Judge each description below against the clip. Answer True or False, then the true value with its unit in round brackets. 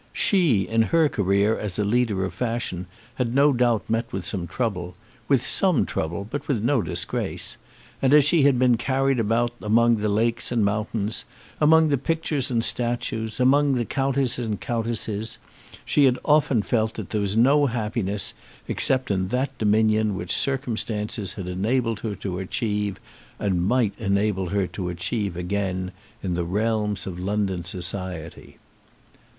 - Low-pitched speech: True (110 Hz)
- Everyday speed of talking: True (160 wpm)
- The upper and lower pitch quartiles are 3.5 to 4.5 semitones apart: True (4.1 semitones)